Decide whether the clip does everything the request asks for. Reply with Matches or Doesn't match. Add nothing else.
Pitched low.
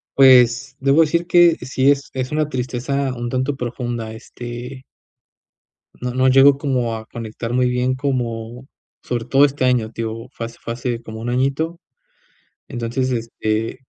Matches